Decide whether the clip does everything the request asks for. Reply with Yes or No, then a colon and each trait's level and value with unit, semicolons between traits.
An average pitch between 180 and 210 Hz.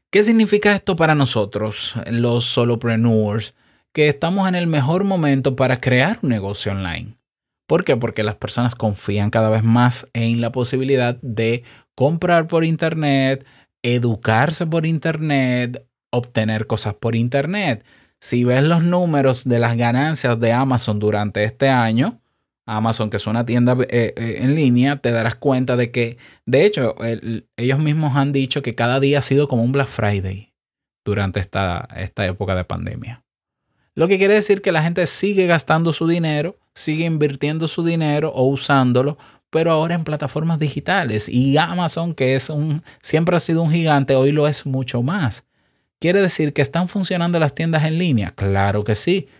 No: low, 130 Hz